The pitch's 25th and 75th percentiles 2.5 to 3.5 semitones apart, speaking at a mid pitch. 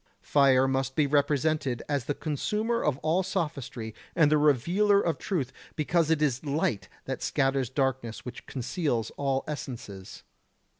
Yes: average, 3.2 semitones; medium, 145 Hz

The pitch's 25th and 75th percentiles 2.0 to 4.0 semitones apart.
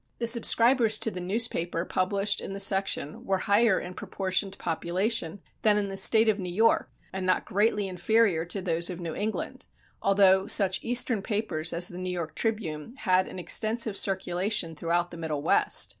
Yes: average, 3.5 semitones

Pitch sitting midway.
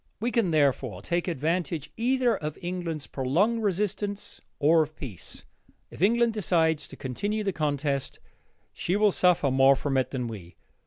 Yes: medium, 165 Hz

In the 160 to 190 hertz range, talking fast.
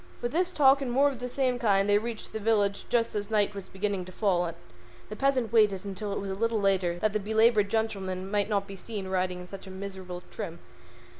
No: high, 205 Hz; fast, 235 wpm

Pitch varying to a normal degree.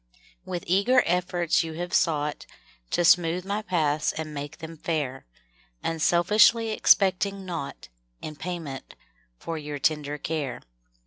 Yes: average, 3.2 semitones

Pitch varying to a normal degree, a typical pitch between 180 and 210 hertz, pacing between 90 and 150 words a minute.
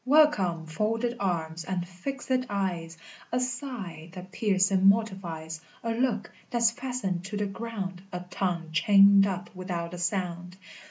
Yes: average, 4.4 semitones; high, 190 Hz; average, 140 wpm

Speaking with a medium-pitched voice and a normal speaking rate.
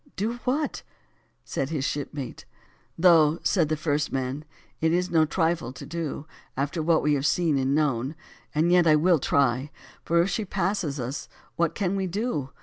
Yes: medium, 155 Hz; average, 170 wpm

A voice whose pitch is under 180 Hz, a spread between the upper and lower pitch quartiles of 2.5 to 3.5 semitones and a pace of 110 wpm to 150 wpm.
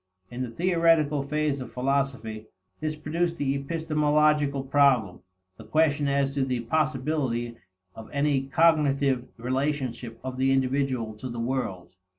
Yes: medium, 140 Hz; average, 3.1 semitones; slow, 135 wpm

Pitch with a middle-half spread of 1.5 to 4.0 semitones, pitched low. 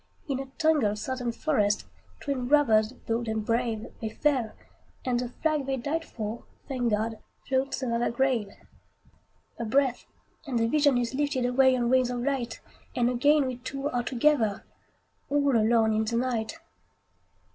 No: average, 3.1 semitones; high, 245 Hz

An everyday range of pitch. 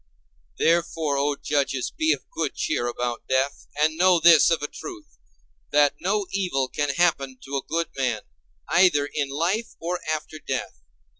Yes: average, 4.1 semitones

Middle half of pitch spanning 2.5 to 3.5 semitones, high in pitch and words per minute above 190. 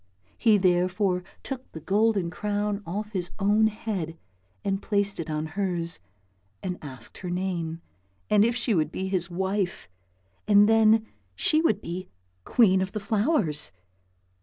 No: average, 3.2 semitones; high, 195 Hz; average, 145 wpm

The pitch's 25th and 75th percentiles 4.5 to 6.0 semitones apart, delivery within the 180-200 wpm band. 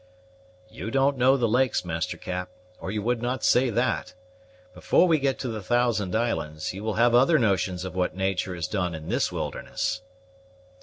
Yes: average, 5.2 semitones; average, 185 wpm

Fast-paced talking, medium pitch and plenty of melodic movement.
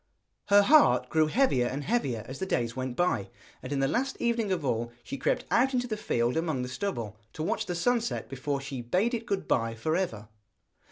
Yes: fast, 220 wpm; medium, 150 Hz; wide, 8.9 semitones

